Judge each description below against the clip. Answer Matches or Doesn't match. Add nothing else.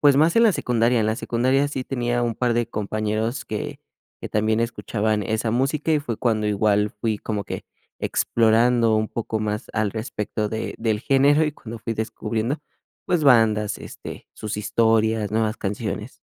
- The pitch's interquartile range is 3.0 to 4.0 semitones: Doesn't match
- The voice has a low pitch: Matches